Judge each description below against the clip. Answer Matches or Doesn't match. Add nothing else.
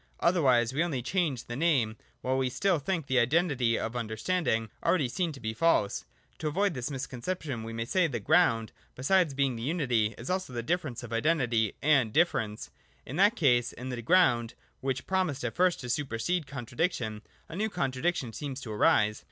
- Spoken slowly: Doesn't match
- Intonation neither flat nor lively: Doesn't match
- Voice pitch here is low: Matches